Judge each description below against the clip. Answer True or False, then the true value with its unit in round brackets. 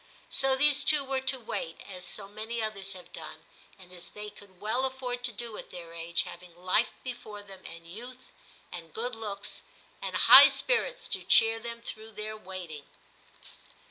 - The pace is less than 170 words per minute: False (180 wpm)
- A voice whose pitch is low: False (215 Hz)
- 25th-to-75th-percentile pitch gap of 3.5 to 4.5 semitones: False (5.0 semitones)